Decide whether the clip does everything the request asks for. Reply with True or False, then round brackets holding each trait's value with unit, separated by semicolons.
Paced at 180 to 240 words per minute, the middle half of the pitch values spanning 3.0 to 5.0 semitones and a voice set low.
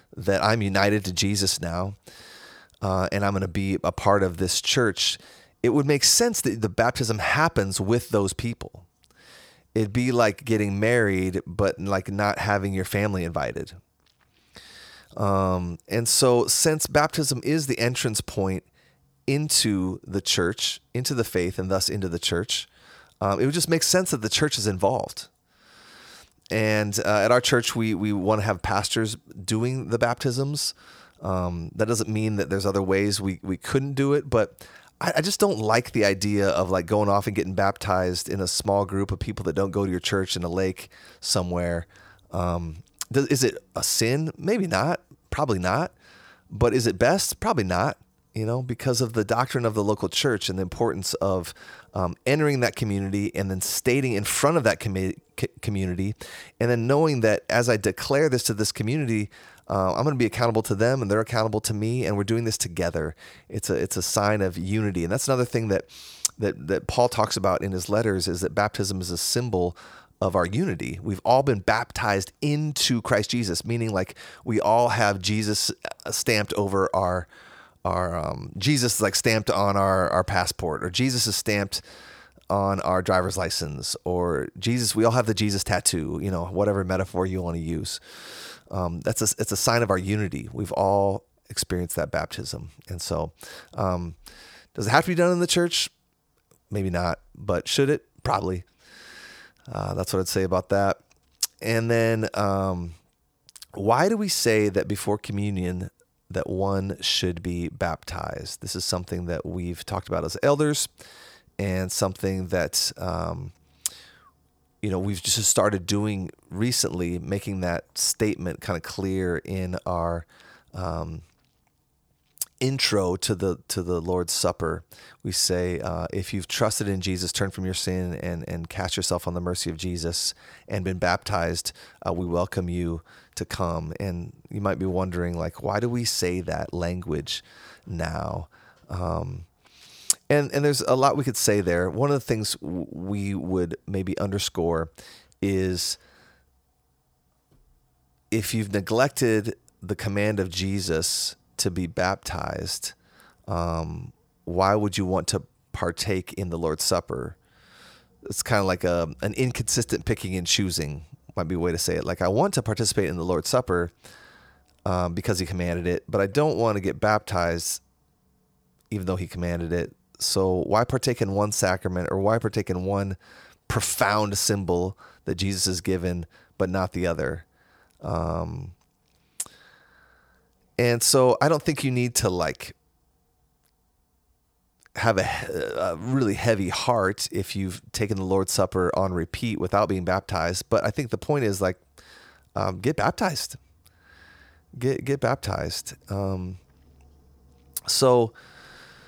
False (170 wpm; 3.8 semitones; 100 Hz)